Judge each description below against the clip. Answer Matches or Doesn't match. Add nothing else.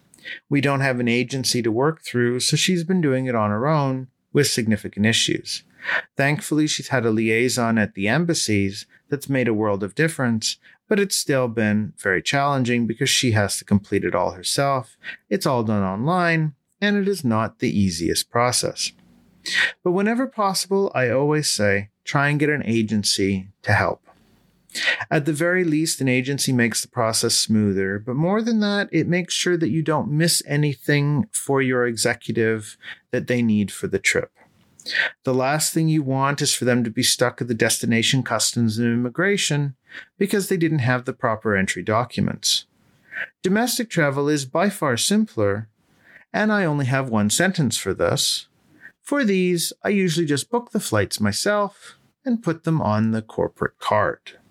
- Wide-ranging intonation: Matches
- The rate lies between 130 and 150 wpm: Doesn't match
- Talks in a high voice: Doesn't match